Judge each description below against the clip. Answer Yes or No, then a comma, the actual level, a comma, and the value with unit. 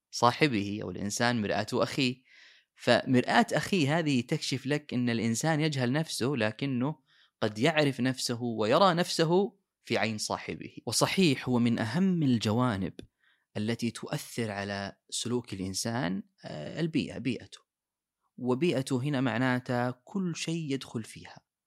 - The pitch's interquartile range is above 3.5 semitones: Yes, average, 5.0 semitones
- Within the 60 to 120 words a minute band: Yes, average, 115 wpm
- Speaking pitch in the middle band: No, low, 125 Hz